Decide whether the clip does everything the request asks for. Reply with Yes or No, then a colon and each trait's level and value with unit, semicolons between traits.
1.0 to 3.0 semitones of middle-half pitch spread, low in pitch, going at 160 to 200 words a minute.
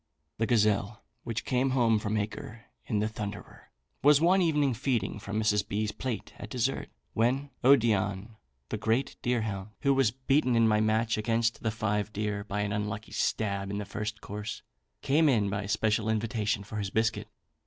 Yes: narrow, 2.5 semitones; low, 110 Hz; average, 175 wpm